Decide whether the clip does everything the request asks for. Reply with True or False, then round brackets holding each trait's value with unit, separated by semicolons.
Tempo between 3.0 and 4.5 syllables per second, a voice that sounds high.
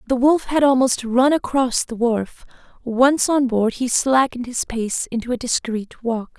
True (4.4 syllables/s; 245 Hz)